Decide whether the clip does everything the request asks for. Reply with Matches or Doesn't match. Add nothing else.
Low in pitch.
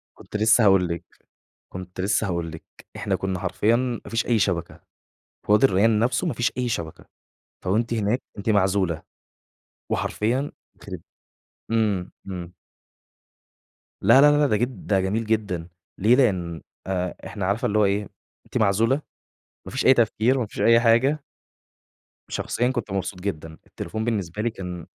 Matches